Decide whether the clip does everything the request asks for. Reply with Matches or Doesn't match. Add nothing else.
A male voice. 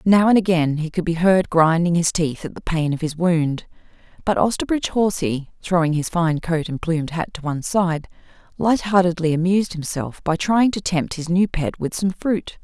Doesn't match